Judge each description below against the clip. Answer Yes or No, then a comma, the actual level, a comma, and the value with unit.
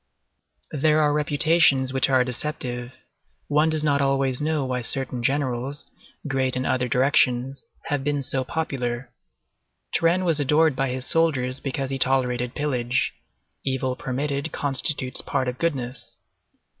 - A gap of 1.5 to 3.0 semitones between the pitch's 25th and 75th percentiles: Yes, narrow, 2.5 semitones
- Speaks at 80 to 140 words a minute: Yes, slow, 135 wpm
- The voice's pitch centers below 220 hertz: Yes, low, 135 Hz